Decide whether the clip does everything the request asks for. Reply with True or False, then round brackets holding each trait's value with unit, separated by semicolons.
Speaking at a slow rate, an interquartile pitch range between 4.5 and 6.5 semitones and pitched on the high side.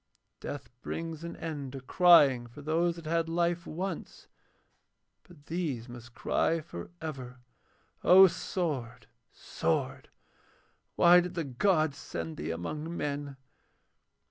False (120 wpm; 4.8 semitones; 155 Hz)